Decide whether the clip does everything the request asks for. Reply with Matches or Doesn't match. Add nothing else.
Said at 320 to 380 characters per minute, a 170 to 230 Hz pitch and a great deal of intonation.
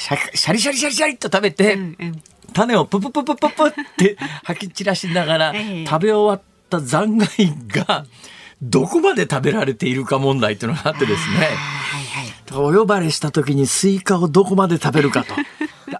Matches